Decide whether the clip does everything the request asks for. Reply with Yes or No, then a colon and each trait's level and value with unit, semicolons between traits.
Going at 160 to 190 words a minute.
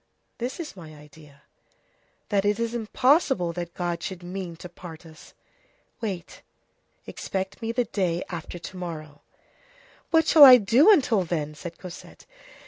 No: average, 145 wpm